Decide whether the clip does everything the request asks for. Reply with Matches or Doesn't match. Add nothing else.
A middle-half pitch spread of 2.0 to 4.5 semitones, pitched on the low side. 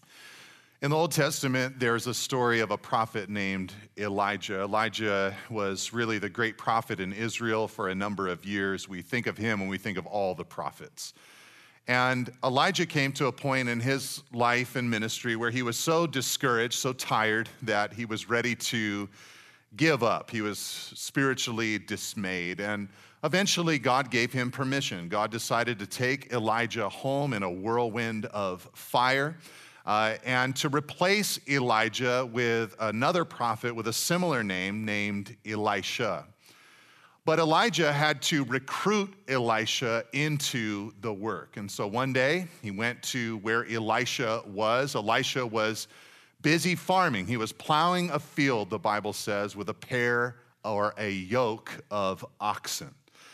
Matches